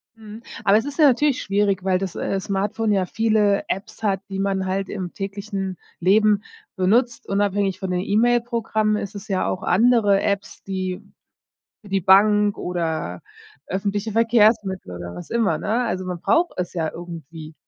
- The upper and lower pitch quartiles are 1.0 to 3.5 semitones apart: Yes, narrow, 2.5 semitones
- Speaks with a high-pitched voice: Yes, high, 200 Hz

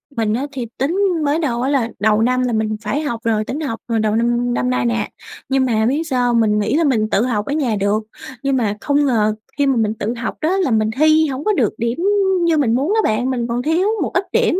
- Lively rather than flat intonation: No, average, 4.6 semitones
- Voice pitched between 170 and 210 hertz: No, high, 240 Hz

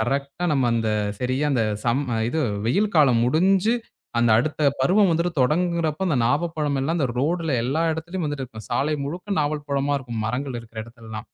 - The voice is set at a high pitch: No, medium, 140 Hz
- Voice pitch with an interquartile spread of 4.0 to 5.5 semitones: Yes, average, 5.0 semitones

